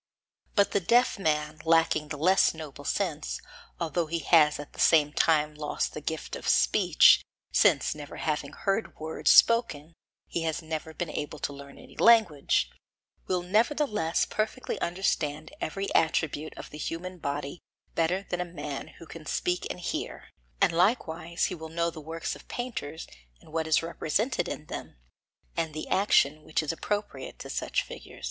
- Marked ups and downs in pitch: No, average, 3.2 semitones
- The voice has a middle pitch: Yes, medium, 160 Hz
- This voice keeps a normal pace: Yes, average, 165 wpm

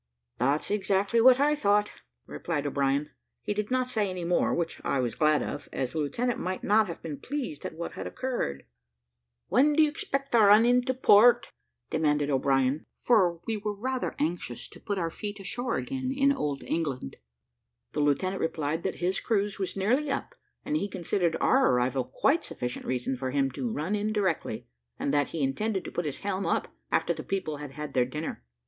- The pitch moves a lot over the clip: Yes, wide, 7.9 semitones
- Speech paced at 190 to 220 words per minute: Yes, average, 195 wpm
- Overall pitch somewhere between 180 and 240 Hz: Yes, medium, 185 Hz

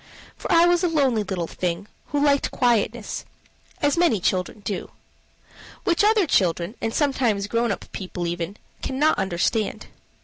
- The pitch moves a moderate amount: No, wide, 7.2 semitones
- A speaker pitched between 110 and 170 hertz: No, high, 225 Hz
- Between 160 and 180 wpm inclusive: No, average, 145 wpm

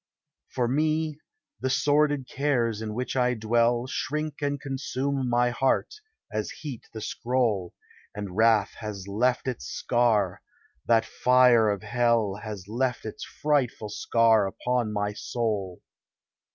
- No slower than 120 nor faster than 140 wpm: Yes, slow, 135 wpm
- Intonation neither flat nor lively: Yes, average, 3.5 semitones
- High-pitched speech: No, low, 120 Hz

